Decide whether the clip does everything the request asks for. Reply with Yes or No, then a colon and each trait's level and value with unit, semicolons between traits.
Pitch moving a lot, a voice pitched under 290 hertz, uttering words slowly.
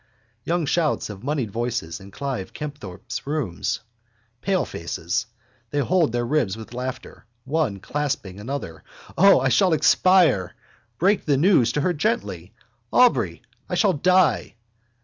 Yes: wide, 7.1 semitones; medium, 140 Hz; slow, 130 wpm